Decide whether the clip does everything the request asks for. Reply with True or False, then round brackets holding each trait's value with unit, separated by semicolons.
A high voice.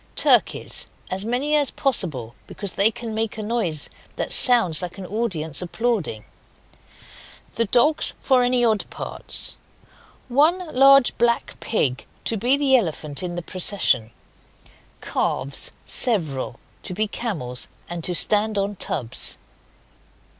True (210 Hz)